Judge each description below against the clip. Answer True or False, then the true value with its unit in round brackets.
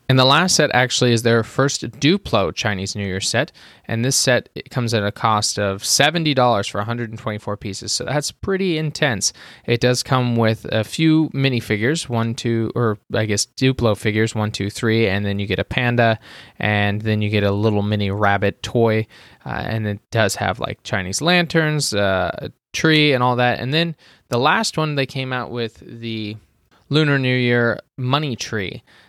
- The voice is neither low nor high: False (115 Hz)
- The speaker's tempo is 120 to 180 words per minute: False (190 wpm)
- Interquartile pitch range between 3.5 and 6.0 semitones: True (4.2 semitones)